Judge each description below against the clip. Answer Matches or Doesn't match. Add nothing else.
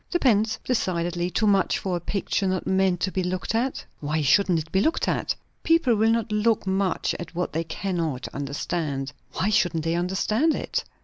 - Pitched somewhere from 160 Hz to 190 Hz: Matches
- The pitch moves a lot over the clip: Doesn't match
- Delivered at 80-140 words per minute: Doesn't match